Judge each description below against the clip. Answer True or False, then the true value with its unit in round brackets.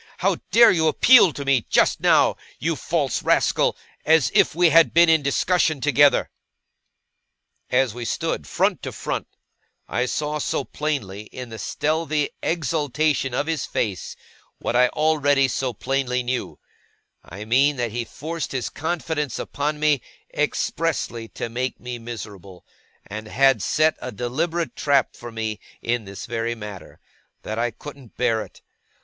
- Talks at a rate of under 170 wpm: True (150 wpm)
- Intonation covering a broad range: False (4.6 semitones)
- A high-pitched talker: False (135 Hz)